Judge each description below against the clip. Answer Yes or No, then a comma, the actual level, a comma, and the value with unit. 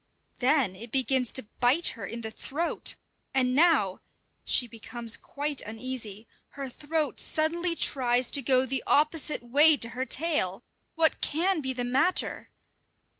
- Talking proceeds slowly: No, average, 145 wpm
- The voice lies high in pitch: Yes, very high, 260 Hz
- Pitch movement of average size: Yes, average, 4.2 semitones